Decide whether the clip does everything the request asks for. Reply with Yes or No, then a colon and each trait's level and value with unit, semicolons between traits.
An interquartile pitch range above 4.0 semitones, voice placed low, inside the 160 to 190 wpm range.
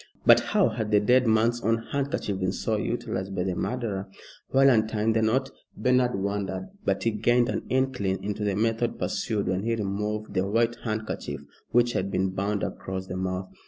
No: average, 3.4 semitones; low, 110 Hz; average, 185 wpm